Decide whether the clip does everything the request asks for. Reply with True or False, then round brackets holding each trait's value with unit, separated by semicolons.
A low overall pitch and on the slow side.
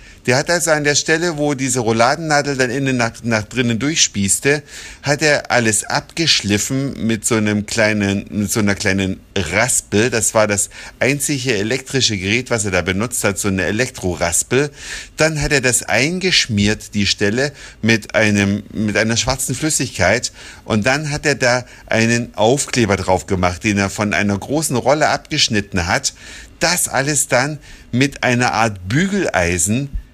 False (115 Hz; 155 wpm)